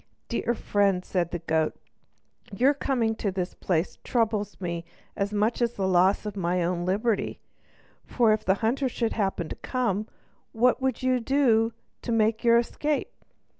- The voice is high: Yes, high, 215 Hz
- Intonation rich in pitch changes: No, average, 4.1 semitones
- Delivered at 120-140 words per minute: No, average, 165 wpm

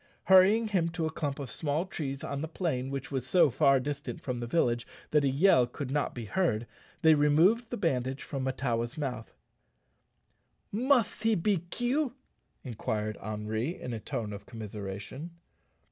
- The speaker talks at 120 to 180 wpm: Yes, average, 165 wpm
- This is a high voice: No, medium, 140 Hz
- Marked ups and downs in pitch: Yes, wide, 6.3 semitones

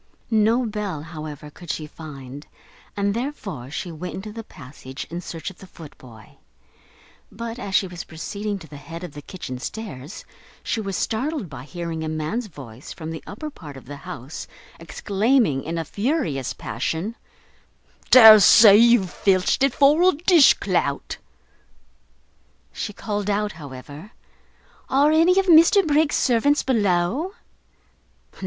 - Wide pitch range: Yes, wide, 7.2 semitones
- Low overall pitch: No, high, 190 Hz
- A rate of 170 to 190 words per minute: No, average, 150 wpm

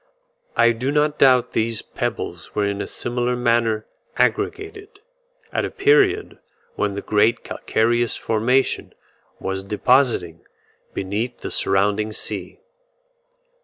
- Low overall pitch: Yes, low, 115 Hz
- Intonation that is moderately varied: Yes, average, 3.8 semitones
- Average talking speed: No, slow, 115 wpm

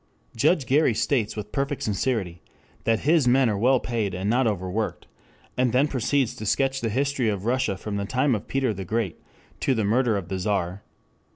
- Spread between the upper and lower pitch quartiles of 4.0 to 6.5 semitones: Yes, average, 4.6 semitones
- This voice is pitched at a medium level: No, low, 115 Hz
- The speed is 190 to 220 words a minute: Yes, average, 195 wpm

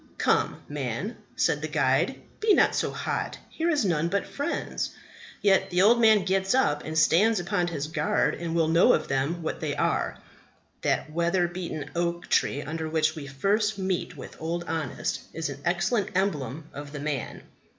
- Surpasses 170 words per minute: Yes, average, 180 wpm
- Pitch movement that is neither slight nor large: Yes, average, 3.7 semitones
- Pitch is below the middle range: No, medium, 170 Hz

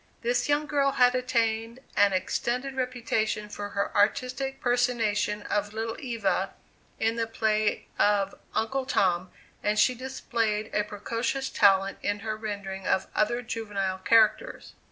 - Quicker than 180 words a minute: No, slow, 135 wpm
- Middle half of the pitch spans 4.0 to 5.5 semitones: No, average, 3.2 semitones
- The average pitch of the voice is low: No, high, 220 Hz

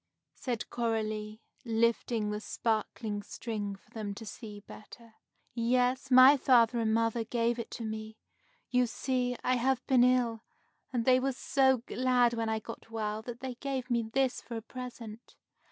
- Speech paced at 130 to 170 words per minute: Yes, average, 165 wpm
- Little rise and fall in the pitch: Yes, narrow, 2.3 semitones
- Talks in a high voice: Yes, high, 235 Hz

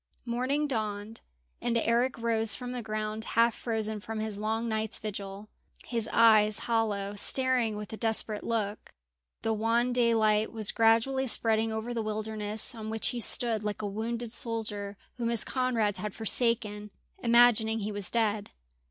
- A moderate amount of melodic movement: No, narrow, 1.6 semitones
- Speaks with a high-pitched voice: Yes, high, 220 Hz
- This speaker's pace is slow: No, average, 155 wpm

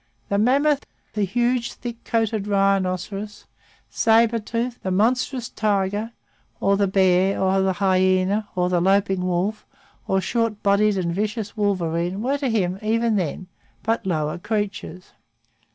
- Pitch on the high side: Yes, high, 200 Hz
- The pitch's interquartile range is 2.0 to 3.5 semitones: Yes, average, 3.2 semitones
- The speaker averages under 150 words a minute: Yes, slow, 135 wpm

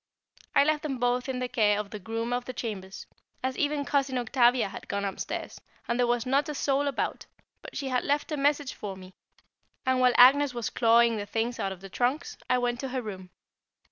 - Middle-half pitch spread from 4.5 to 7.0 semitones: No, average, 3.4 semitones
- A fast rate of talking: Yes, fast, 220 wpm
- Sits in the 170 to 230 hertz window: No, high, 245 Hz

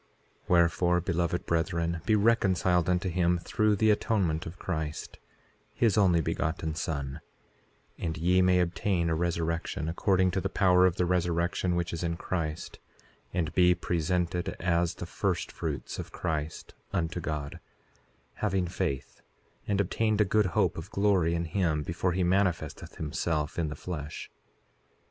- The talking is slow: No, average, 150 wpm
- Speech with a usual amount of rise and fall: No, narrow, 2.1 semitones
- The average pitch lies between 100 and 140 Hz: No, very low, 85 Hz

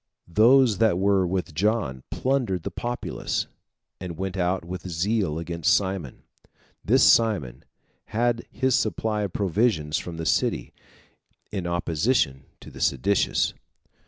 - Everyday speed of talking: No, slow, 130 wpm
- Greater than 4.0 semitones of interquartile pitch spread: Yes, average, 4.7 semitones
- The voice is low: Yes, very low, 95 Hz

